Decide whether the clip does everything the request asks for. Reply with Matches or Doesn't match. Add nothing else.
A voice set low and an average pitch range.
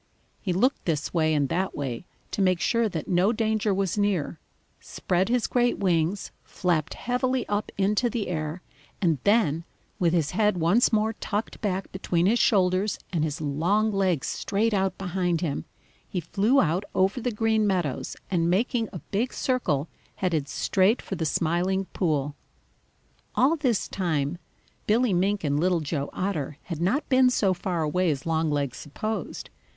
Doesn't match